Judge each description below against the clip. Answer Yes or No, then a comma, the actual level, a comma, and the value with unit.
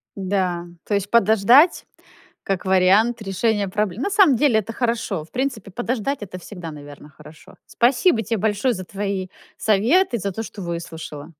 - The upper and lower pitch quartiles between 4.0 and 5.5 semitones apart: Yes, average, 4.3 semitones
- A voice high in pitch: Yes, high, 205 Hz